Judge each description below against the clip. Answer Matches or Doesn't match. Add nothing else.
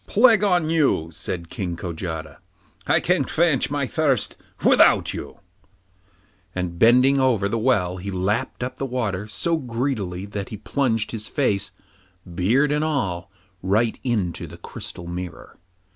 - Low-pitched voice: Matches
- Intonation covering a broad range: Matches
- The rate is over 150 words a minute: Doesn't match